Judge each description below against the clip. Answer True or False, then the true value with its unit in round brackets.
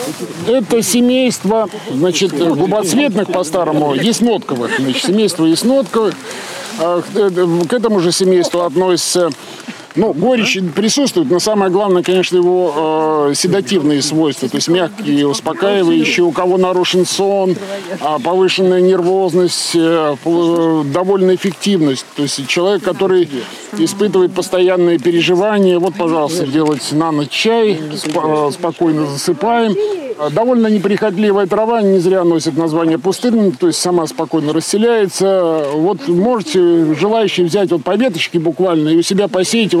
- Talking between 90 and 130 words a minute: True (115 wpm)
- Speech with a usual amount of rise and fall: True (3.4 semitones)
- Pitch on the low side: False (180 Hz)